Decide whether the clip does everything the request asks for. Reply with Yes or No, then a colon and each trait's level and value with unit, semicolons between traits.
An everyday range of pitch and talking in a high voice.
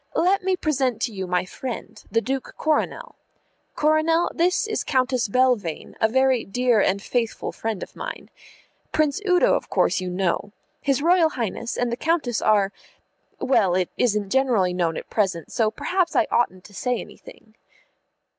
No: wide, 7.0 semitones; high, 245 Hz